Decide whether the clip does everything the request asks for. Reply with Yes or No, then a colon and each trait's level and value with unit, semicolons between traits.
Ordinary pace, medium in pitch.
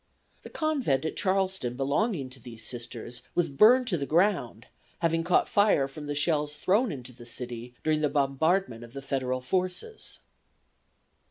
Yes: average, 160 wpm; medium, 145 Hz